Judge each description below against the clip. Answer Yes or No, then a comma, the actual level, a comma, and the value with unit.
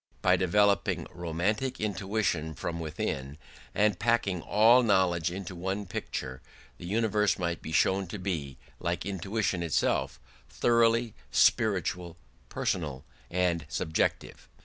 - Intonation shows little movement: No, average, 3.7 semitones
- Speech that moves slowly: Yes, slow, 115 wpm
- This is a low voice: Yes, very low, 90 Hz